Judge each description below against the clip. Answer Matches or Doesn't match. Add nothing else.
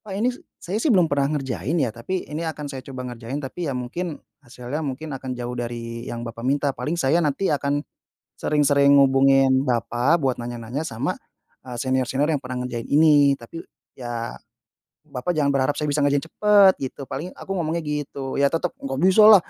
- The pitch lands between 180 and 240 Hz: Doesn't match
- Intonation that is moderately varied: Matches